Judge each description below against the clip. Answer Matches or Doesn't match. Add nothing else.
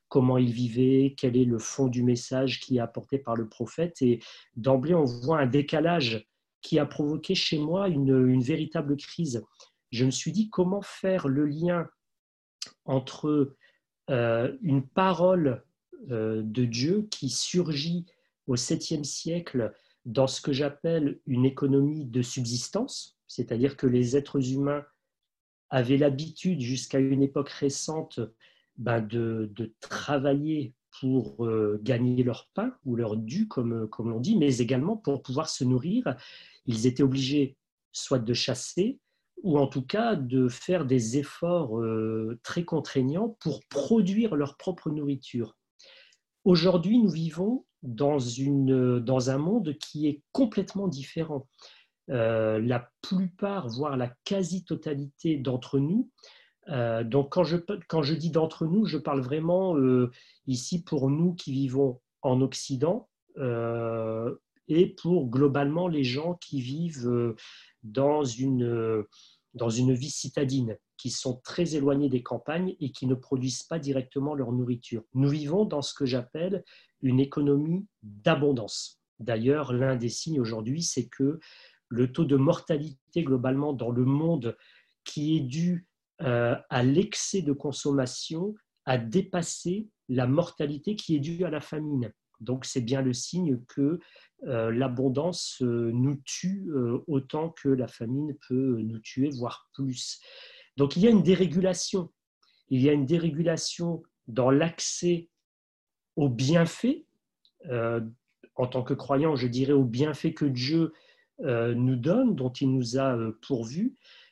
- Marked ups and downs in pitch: Doesn't match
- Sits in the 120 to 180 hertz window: Matches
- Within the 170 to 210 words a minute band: Doesn't match